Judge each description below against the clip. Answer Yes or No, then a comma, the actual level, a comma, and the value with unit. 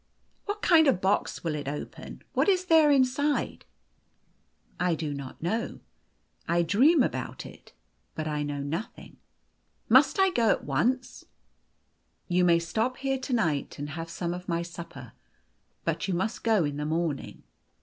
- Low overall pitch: No, medium, 180 Hz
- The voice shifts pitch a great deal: Yes, wide, 8.4 semitones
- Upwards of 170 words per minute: Yes, average, 180 wpm